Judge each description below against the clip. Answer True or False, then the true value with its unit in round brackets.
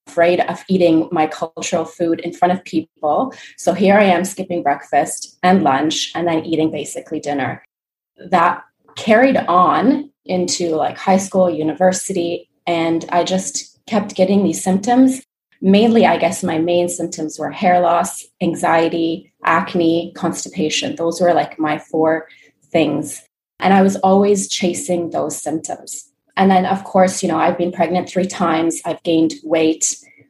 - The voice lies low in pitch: False (175 Hz)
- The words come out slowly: False (155 wpm)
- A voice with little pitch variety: True (2.2 semitones)